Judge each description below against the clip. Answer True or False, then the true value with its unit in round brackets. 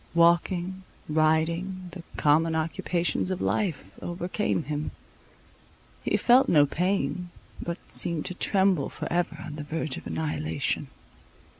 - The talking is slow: True (125 wpm)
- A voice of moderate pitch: True (170 Hz)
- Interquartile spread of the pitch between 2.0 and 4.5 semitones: True (2.8 semitones)